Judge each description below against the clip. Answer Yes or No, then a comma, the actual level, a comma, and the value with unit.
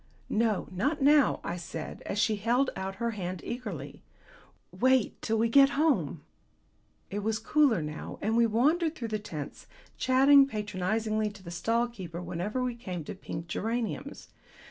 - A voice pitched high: Yes, high, 220 Hz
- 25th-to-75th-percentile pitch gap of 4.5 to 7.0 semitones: Yes, average, 5.2 semitones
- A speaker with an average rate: Yes, average, 160 wpm